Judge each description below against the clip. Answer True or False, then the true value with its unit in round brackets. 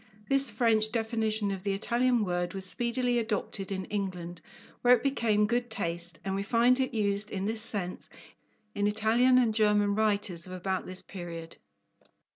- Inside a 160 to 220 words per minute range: True (165 wpm)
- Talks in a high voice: True (210 Hz)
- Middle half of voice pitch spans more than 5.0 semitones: False (3.5 semitones)